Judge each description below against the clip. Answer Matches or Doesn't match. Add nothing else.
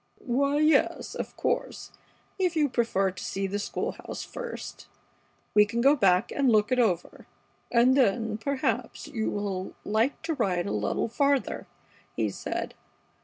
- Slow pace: Doesn't match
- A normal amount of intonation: Doesn't match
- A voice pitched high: Matches